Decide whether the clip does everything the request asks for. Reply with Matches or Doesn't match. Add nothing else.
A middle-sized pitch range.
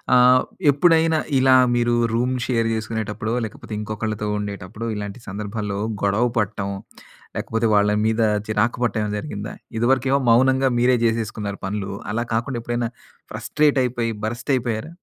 Matches